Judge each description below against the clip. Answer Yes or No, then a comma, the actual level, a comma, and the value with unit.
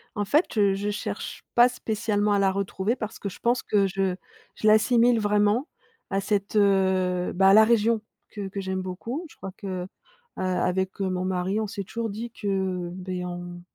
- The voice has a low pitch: No, high, 200 Hz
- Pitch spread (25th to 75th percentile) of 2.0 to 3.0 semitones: Yes, narrow, 2.4 semitones